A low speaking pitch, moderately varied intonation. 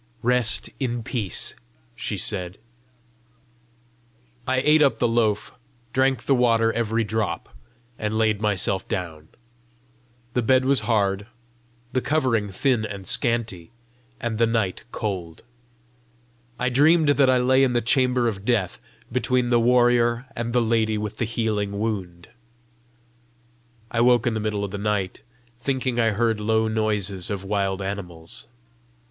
Yes: low, 115 Hz; average, 3.3 semitones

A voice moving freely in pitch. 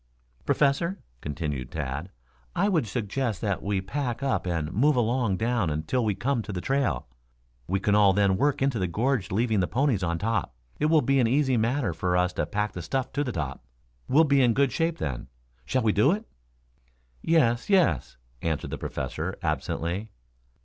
Yes: wide, 7.0 semitones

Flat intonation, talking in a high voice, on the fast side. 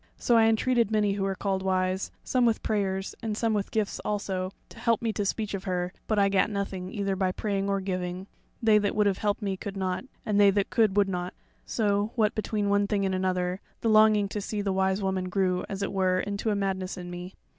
Yes: narrow, 2.0 semitones; high, 200 Hz; fast, 235 wpm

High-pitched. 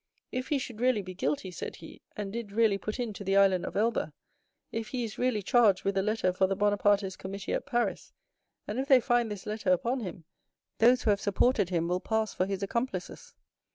Yes: high, 205 Hz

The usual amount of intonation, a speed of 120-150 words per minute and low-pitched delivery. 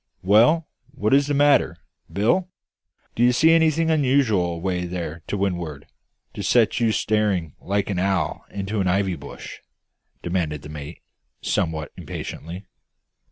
No: wide, 6.0 semitones; average, 140 wpm; low, 100 Hz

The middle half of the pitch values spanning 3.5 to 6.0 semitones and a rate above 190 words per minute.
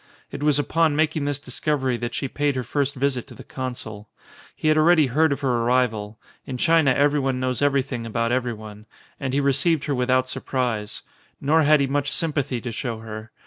No: average, 3.1 semitones; fast, 205 wpm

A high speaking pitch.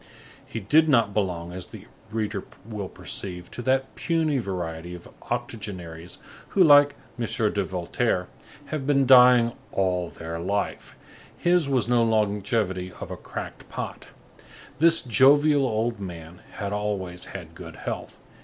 No: low, 105 Hz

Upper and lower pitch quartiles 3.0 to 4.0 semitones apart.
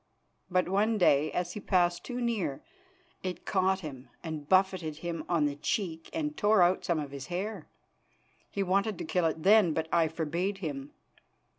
Yes: average, 3.7 semitones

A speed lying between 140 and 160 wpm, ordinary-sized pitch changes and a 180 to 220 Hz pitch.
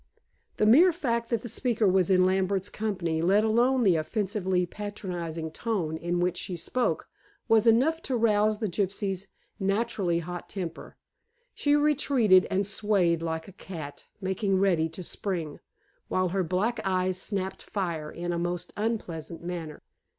Yes: average, 155 wpm; average, 3.7 semitones; high, 190 Hz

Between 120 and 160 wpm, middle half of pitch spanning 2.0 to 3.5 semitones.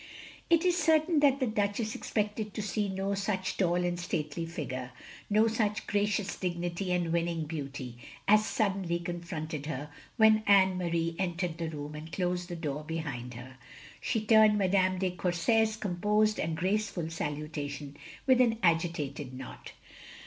No: average, 155 wpm; average, 4.7 semitones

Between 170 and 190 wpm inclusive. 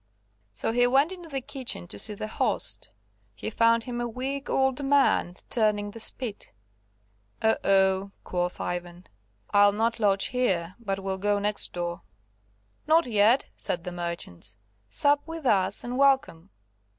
No: average, 150 wpm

